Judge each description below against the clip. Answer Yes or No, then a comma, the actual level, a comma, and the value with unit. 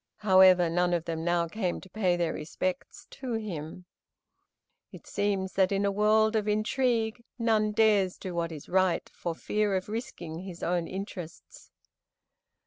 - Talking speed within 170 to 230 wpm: No, average, 155 wpm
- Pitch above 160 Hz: Yes, high, 190 Hz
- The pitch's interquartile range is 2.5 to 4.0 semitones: Yes, average, 3.5 semitones